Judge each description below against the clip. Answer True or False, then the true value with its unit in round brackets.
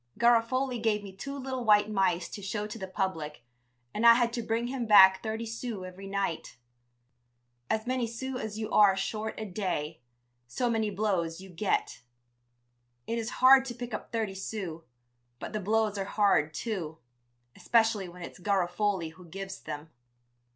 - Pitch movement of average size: True (3.4 semitones)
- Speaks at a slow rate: False (170 wpm)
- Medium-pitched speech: False (210 Hz)